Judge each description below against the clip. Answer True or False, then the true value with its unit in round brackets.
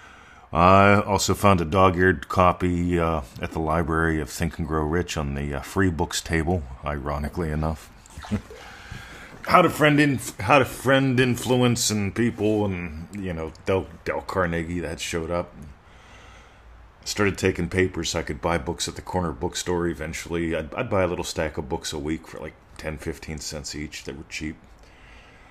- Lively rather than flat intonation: False (3.1 semitones)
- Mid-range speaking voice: False (85 Hz)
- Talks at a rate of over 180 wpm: False (170 wpm)